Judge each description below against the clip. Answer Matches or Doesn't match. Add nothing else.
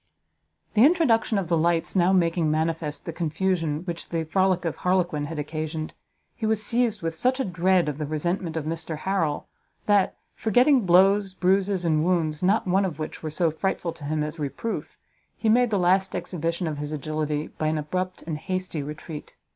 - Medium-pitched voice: Matches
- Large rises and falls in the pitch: Doesn't match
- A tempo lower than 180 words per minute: Doesn't match